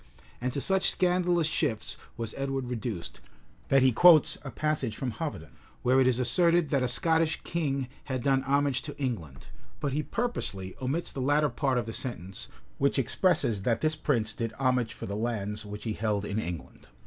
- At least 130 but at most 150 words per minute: No, average, 185 wpm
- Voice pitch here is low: Yes, low, 130 Hz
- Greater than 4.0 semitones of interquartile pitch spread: Yes, average, 4.9 semitones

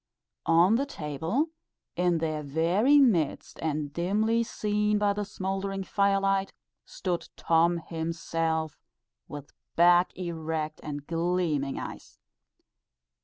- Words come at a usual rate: No, slow, 105 wpm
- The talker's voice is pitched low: No, medium, 175 Hz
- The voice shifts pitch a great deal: No, average, 3.6 semitones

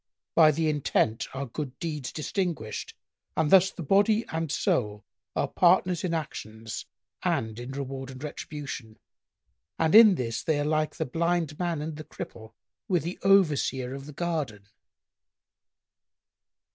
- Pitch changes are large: No, average, 4.5 semitones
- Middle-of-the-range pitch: Yes, medium, 150 Hz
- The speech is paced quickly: No, average, 145 wpm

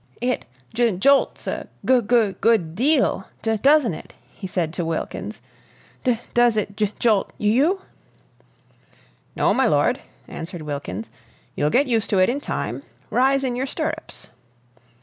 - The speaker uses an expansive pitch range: Yes, wide, 5.7 semitones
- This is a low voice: No, high, 225 Hz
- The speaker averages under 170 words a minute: Yes, average, 150 wpm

